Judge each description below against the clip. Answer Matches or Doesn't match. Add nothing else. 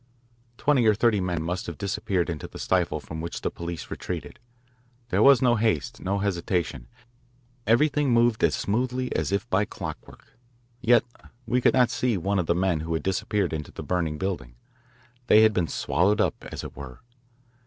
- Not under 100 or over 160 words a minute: Doesn't match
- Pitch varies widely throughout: Matches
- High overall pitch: Doesn't match